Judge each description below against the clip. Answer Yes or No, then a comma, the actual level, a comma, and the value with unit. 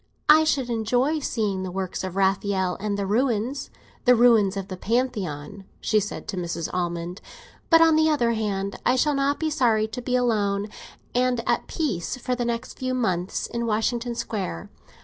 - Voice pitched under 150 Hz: No, high, 225 Hz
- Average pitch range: Yes, average, 4.5 semitones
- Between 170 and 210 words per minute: Yes, average, 175 wpm